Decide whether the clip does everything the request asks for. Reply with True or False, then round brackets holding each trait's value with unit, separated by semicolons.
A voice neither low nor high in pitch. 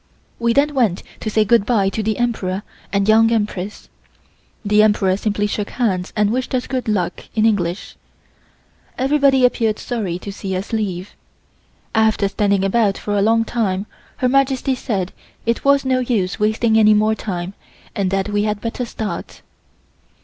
False (215 Hz)